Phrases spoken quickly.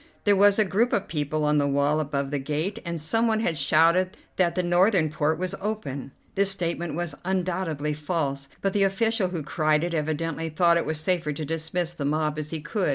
Yes: fast, 210 wpm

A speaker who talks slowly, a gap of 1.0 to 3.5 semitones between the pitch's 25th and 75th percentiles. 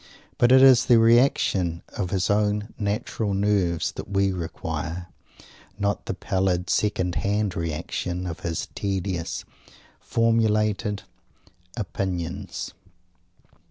Yes: slow, 105 wpm; average, 3.0 semitones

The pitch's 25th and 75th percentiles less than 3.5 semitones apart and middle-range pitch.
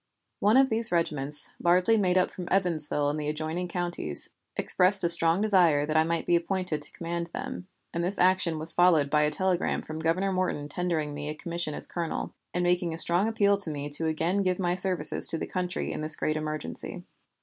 Yes: average, 3.0 semitones; medium, 170 Hz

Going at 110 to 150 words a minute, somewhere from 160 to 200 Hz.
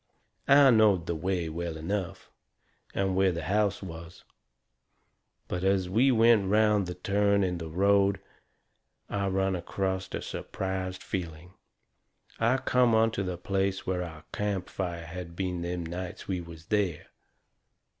No: average, 140 wpm; very low, 95 Hz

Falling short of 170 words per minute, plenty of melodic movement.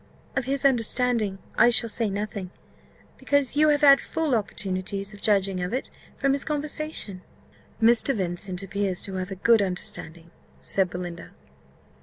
Yes: average, 150 wpm; wide, 5.9 semitones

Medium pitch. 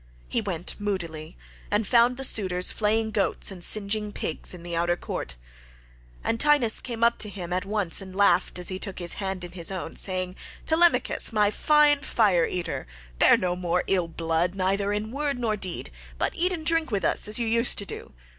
No: high, 200 Hz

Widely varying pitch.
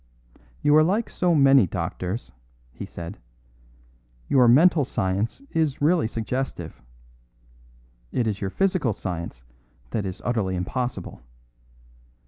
Yes: wide, 7.7 semitones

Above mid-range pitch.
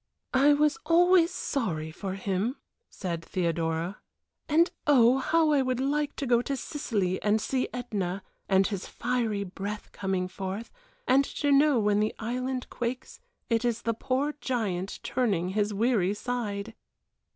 Yes: high, 230 Hz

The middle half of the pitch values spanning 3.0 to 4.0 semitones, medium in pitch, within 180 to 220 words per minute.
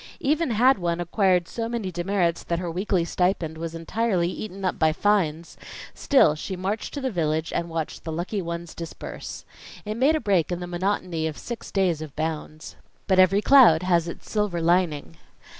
Yes: average, 3.6 semitones; medium, 175 Hz; average, 185 wpm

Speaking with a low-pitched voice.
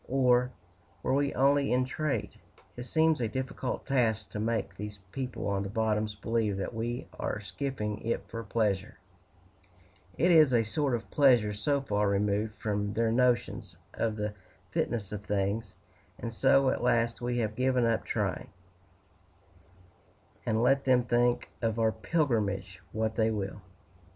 Yes: low, 115 Hz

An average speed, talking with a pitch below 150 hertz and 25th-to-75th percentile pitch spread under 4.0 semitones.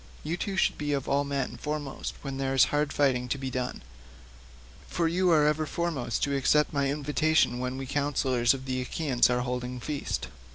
Yes: average, 195 wpm; medium, 140 Hz; average, 2.8 semitones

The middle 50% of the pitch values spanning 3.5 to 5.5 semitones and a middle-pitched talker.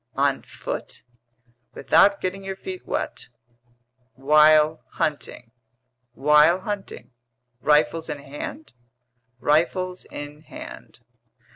Yes: average, 4.1 semitones; medium, 155 Hz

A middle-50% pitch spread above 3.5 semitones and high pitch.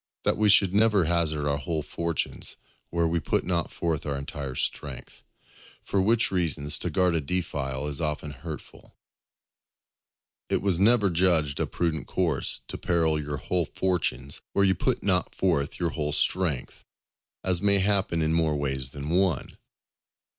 No: average, 3.9 semitones; very low, 85 Hz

